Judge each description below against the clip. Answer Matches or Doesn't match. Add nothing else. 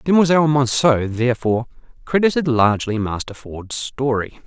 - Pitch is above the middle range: Doesn't match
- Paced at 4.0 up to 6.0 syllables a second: Matches